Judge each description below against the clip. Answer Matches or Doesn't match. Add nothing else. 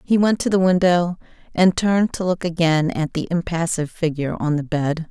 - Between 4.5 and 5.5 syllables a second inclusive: Matches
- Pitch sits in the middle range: Matches